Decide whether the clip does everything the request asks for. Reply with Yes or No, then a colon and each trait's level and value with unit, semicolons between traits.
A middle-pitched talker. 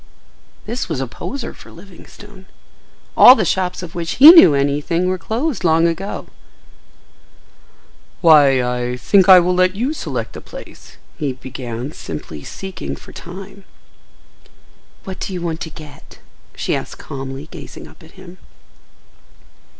Yes: medium, 170 Hz